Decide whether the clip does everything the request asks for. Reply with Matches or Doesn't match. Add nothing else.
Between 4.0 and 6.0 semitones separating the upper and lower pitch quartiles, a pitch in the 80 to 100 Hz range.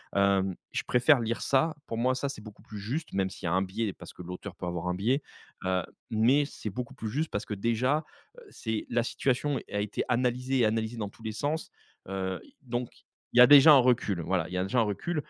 Doesn't match